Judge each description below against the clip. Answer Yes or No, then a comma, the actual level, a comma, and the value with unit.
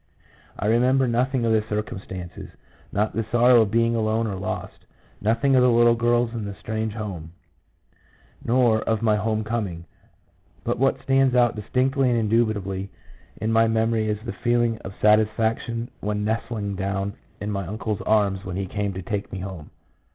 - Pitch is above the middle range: No, low, 110 Hz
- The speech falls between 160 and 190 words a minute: Yes, average, 175 wpm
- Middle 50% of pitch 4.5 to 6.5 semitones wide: No, narrow, 2.6 semitones